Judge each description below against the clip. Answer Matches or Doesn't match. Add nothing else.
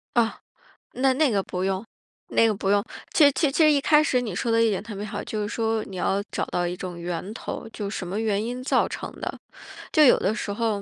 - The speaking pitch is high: Matches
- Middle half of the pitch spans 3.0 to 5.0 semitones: Matches